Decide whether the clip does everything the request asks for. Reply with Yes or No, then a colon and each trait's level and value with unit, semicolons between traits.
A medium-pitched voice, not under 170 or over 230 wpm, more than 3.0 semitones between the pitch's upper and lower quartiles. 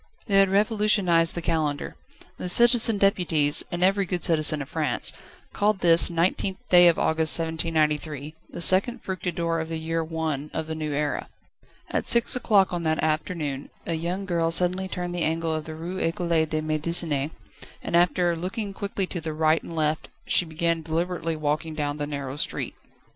No: medium, 165 Hz; average, 175 wpm; narrow, 2.5 semitones